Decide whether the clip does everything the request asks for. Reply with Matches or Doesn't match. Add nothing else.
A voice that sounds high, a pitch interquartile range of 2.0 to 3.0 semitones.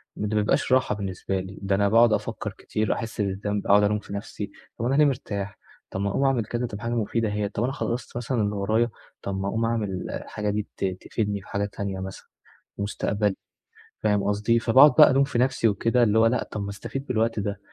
Doesn't match